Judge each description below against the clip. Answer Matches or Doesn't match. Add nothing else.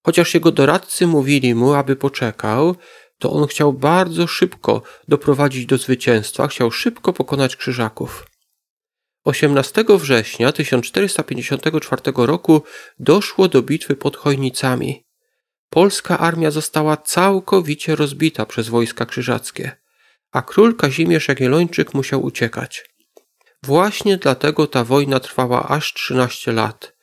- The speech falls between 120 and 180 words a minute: Doesn't match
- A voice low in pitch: Doesn't match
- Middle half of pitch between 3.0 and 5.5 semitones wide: Matches